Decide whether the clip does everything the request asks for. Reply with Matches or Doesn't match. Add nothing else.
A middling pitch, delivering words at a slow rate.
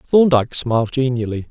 Doesn't match